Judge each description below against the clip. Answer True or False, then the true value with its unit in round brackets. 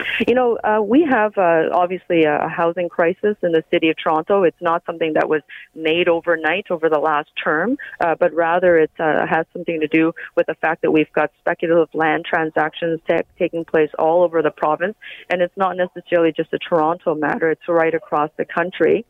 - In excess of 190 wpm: True (200 wpm)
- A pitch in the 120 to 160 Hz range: False (170 Hz)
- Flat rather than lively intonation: True (1.8 semitones)